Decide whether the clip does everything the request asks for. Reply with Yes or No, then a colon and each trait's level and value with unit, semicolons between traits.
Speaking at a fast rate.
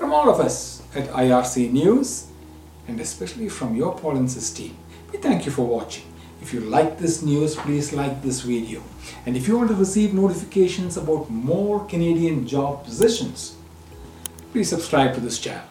No: average, 170 wpm